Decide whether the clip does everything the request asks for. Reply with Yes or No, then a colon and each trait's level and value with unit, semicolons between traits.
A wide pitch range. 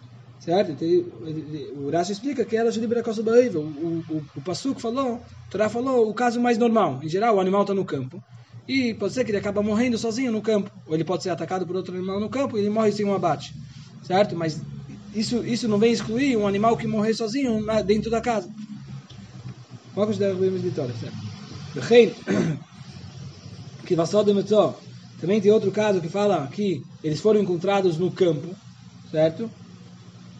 Yes: wide, 6.0 semitones